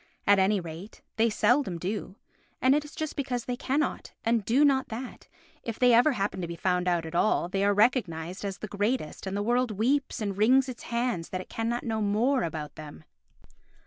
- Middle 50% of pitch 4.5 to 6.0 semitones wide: Yes, average, 4.9 semitones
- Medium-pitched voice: No, high, 215 Hz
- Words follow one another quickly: Yes, fast, 210 wpm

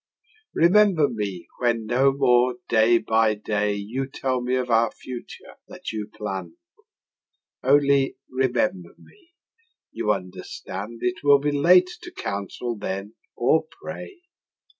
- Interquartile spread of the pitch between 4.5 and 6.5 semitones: Yes, average, 4.9 semitones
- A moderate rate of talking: No, slow, 125 wpm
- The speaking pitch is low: Yes, low, 120 Hz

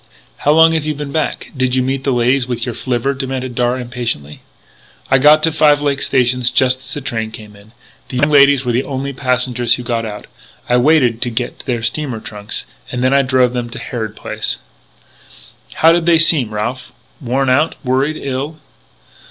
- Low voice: Yes, low, 130 Hz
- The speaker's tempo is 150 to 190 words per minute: No, average, 200 wpm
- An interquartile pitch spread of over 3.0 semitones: No, narrow, 2.5 semitones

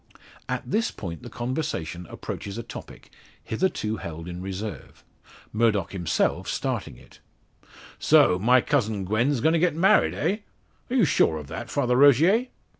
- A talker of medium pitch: No, low, 115 Hz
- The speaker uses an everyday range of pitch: No, wide, 7.7 semitones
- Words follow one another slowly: No, average, 150 wpm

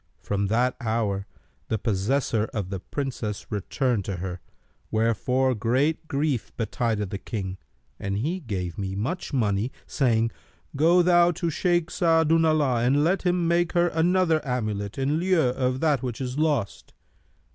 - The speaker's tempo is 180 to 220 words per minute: No, average, 145 wpm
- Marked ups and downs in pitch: Yes, wide, 7.1 semitones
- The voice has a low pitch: Yes, low, 125 Hz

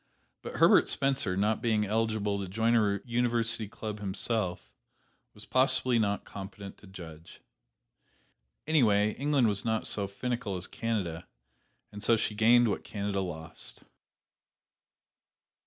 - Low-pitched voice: Yes, low, 105 Hz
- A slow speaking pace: Yes, slow, 125 wpm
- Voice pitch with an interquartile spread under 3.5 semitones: Yes, average, 2.7 semitones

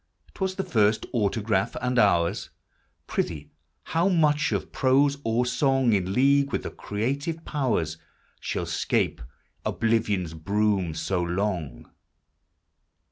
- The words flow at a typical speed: No, slow, 120 wpm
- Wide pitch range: Yes, wide, 6.6 semitones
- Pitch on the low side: Yes, low, 110 Hz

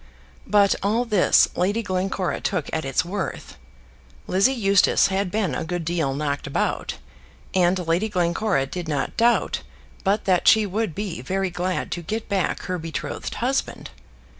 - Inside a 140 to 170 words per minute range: Yes, average, 155 wpm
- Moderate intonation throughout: Yes, average, 3.3 semitones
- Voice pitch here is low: No, medium, 185 Hz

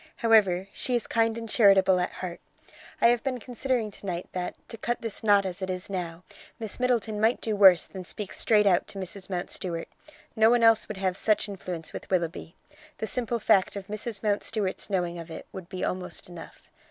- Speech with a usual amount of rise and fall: Yes, average, 3.5 semitones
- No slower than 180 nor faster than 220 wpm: Yes, average, 200 wpm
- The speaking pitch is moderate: No, high, 200 Hz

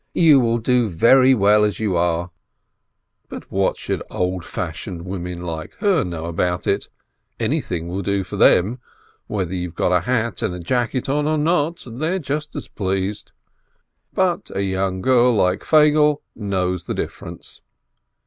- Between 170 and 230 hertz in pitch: No, low, 100 Hz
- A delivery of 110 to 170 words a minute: Yes, average, 150 wpm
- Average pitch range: No, wide, 6.3 semitones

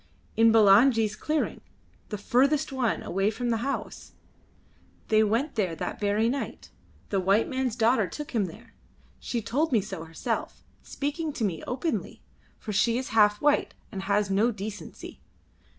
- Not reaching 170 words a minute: Yes, average, 155 wpm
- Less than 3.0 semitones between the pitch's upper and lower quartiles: No, average, 4.2 semitones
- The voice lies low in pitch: No, high, 225 Hz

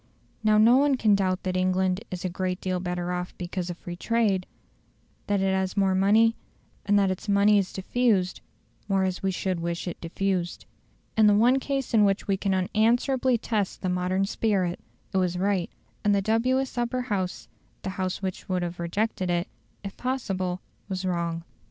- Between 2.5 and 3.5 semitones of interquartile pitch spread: Yes, average, 2.8 semitones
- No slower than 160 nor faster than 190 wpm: Yes, average, 185 wpm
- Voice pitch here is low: No, high, 190 Hz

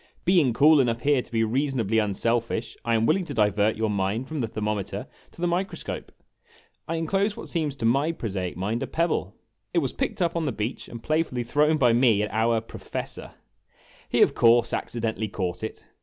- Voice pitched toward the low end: Yes, low, 120 Hz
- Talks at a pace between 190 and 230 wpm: Yes, average, 200 wpm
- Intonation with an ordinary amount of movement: No, wide, 5.8 semitones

